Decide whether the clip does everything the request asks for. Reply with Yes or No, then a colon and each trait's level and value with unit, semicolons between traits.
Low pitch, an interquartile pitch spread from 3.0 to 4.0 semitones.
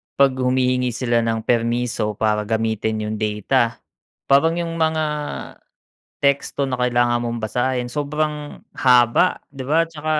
Yes: low, 125 Hz; average, 3.5 semitones